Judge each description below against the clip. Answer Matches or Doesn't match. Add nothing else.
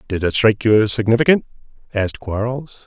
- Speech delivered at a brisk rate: Doesn't match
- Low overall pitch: Matches